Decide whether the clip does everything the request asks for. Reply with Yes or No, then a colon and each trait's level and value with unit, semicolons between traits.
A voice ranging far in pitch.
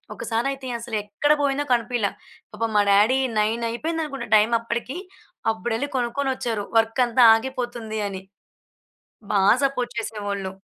No: average, 3.2 semitones